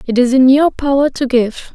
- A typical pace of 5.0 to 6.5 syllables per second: No, 4.8 syllables/s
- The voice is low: No, very high, 260 Hz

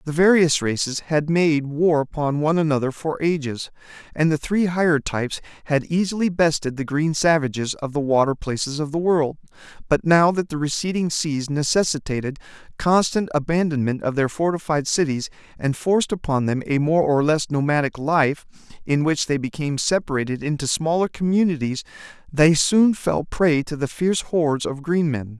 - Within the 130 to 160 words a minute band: No, average, 170 wpm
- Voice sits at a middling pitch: Yes, medium, 155 Hz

